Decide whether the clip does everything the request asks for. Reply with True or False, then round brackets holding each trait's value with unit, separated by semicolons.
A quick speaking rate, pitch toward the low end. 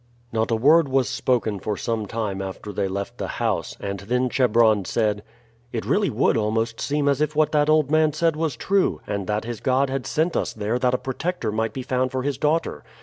True (220 wpm; 125 Hz)